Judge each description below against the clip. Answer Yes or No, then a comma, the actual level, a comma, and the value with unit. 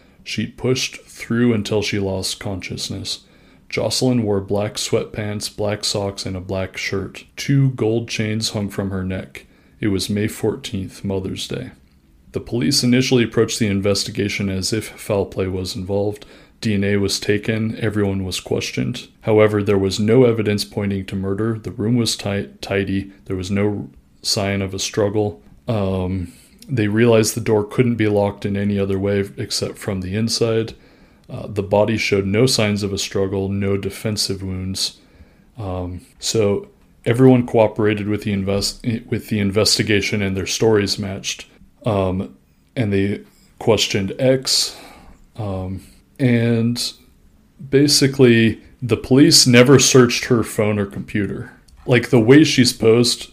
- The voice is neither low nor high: No, low, 105 Hz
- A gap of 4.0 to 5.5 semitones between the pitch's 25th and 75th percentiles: No, average, 3.0 semitones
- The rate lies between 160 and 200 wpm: No, average, 145 wpm